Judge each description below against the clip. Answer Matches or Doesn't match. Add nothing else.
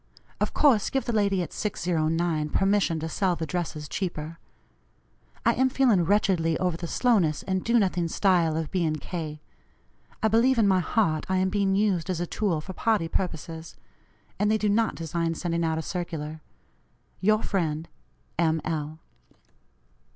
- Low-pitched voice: Doesn't match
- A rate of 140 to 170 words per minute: Matches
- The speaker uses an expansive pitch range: Doesn't match